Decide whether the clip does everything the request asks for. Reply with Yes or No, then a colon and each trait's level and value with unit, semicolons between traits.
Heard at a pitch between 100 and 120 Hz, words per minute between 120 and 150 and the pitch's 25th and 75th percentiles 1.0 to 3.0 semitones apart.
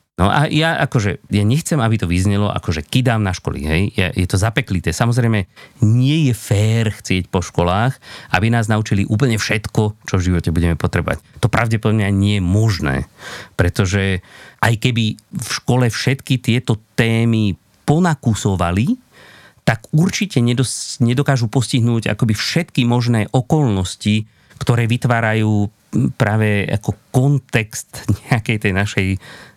No: low, 110 Hz; average, 135 wpm; average, 4.0 semitones